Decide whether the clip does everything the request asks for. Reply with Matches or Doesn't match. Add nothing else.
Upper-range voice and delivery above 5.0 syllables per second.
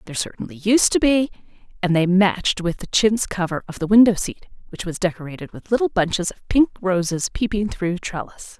Matches